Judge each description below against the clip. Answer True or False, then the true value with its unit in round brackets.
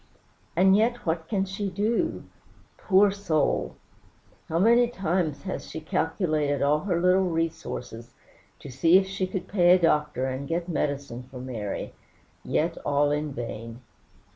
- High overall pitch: False (165 Hz)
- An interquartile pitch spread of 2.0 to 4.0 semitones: False (5.1 semitones)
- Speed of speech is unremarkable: True (145 wpm)